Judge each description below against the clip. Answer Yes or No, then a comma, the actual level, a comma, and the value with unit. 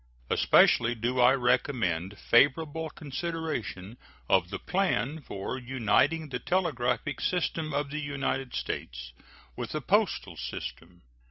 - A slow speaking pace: Yes, slow, 115 wpm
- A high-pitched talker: No, low, 130 Hz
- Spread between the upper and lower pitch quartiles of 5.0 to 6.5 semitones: Yes, average, 5.3 semitones